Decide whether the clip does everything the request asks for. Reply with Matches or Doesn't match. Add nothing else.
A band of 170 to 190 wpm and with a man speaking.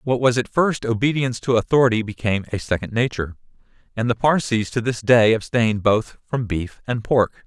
Matches